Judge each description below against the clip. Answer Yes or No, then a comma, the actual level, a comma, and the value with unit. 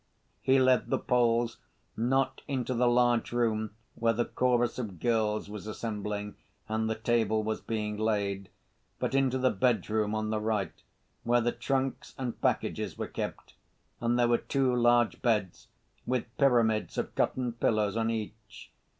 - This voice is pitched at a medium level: No, low, 115 Hz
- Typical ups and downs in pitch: No, narrow, 2.2 semitones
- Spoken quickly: No, average, 155 wpm